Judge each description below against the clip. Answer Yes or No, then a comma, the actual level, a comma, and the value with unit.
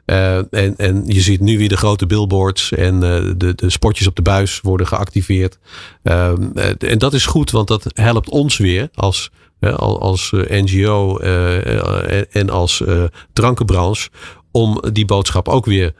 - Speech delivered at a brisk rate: No, average, 165 wpm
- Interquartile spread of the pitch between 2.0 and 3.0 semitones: Yes, narrow, 2.6 semitones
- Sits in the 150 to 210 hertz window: No, very low, 95 Hz